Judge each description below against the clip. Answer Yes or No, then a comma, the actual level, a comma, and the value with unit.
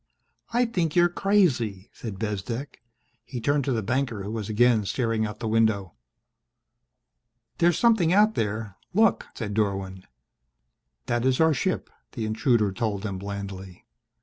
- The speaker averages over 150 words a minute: No, average, 145 wpm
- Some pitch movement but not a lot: No, wide, 6.1 semitones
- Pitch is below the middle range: Yes, low, 115 Hz